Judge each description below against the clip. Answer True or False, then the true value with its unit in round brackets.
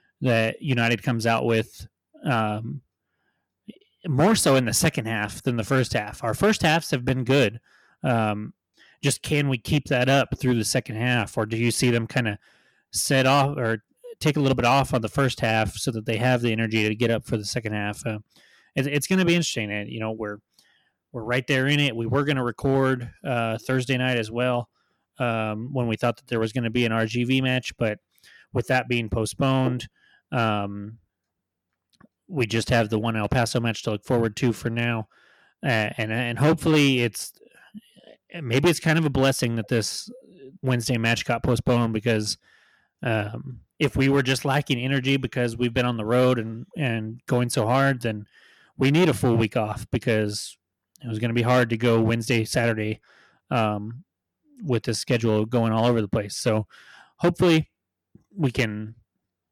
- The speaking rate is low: False (195 wpm)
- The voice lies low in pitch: True (120 Hz)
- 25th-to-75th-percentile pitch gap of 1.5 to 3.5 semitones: True (3.1 semitones)